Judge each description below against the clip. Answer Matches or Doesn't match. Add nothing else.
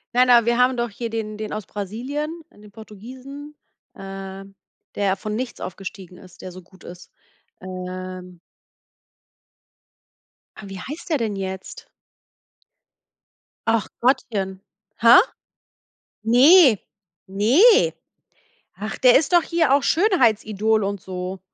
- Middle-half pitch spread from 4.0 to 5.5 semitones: Matches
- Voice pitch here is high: Matches